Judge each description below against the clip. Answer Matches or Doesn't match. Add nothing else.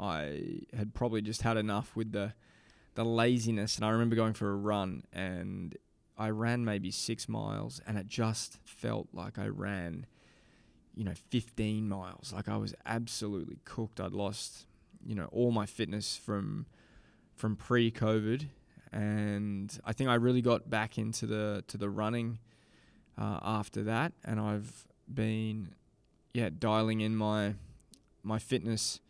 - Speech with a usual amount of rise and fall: Doesn't match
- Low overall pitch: Matches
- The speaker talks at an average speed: Matches